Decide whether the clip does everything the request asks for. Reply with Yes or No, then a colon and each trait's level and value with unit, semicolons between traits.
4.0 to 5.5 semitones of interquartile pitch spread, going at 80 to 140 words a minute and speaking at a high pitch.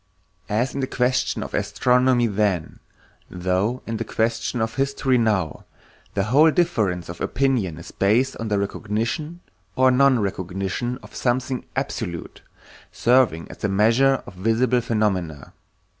No: average, 4.7 semitones; slow, 135 wpm; low, 115 Hz